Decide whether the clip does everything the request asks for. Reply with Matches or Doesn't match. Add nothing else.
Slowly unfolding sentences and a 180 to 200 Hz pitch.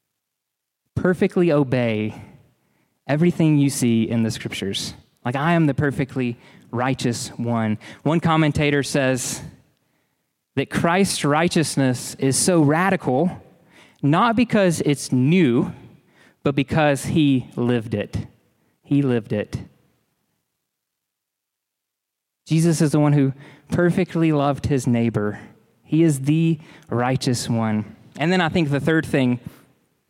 Doesn't match